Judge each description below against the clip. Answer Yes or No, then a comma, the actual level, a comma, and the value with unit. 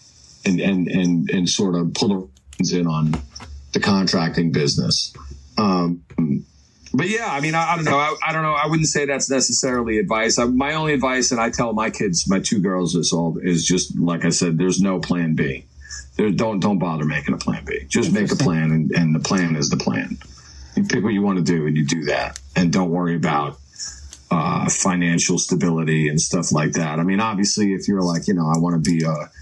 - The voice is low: Yes, very low, 85 Hz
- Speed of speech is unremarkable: No, fast, 220 wpm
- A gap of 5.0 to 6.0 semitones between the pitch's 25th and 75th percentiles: Yes, wide, 5.6 semitones